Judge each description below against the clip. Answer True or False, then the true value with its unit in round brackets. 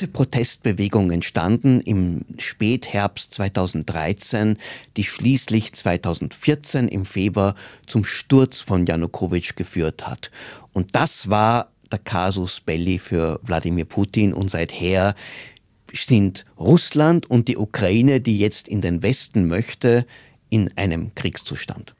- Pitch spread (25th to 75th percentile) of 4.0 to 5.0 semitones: True (4.6 semitones)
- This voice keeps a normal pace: False (110 wpm)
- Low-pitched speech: True (105 Hz)